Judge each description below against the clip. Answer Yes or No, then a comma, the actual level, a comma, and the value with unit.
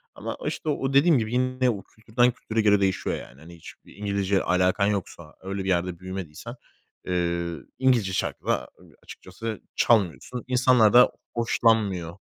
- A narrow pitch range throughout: No, average, 4.6 semitones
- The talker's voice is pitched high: No, low, 100 Hz